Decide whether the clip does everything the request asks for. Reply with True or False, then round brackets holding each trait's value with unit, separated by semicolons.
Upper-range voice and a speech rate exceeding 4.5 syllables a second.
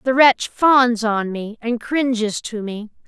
False (230 Hz; 3.6 syllables/s)